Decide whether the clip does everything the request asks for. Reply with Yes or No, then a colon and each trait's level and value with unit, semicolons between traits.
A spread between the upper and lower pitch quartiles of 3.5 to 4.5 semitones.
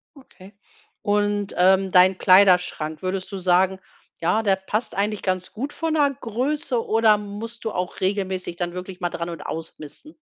No: average, 2.9 semitones